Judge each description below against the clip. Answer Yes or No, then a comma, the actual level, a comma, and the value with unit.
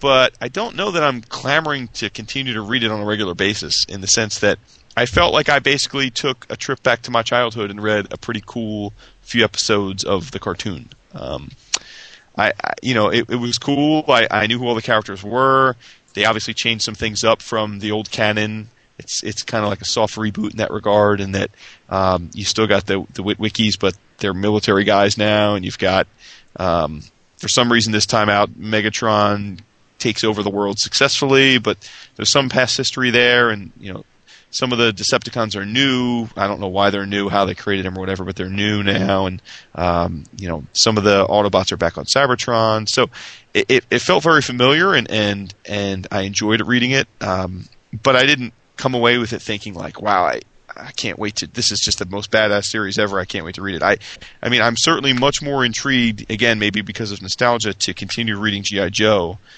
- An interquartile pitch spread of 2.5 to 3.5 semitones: Yes, average, 3.1 semitones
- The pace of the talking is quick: Yes, fast, 215 wpm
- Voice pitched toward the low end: Yes, low, 105 Hz